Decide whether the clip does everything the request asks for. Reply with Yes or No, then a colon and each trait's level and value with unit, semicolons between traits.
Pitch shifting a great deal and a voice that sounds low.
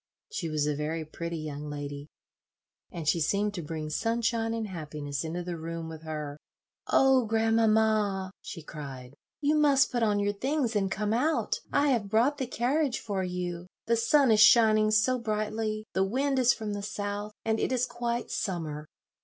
No: wide, 6.1 semitones; high, 210 Hz